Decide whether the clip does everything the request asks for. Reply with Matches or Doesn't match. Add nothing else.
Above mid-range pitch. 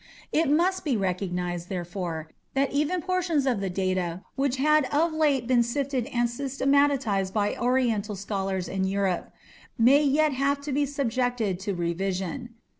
Matches